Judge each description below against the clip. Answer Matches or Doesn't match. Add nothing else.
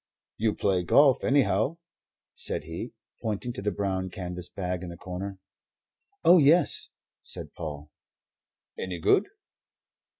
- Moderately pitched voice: Doesn't match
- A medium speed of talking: Doesn't match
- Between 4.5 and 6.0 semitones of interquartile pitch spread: Matches